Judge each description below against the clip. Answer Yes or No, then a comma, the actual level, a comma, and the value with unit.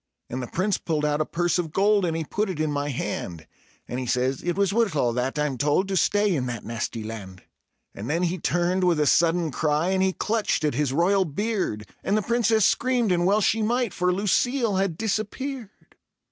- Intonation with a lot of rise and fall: Yes, wide, 5.8 semitones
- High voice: No, medium, 175 Hz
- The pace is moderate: No, fast, 215 wpm